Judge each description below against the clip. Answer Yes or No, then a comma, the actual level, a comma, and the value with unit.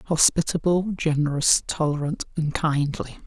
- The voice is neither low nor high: Yes, medium, 155 Hz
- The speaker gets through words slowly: Yes, slow, 90 wpm